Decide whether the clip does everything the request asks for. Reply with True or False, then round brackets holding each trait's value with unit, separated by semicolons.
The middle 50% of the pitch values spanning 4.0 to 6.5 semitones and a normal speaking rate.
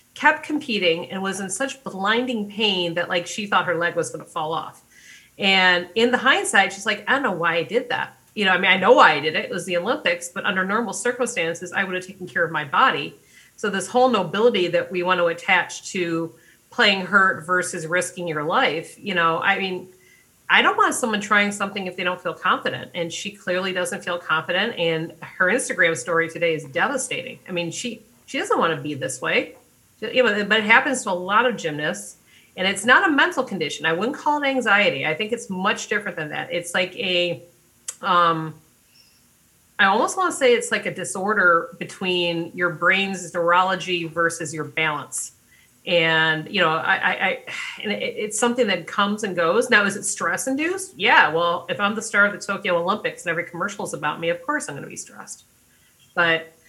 False (4.3 semitones; 215 wpm)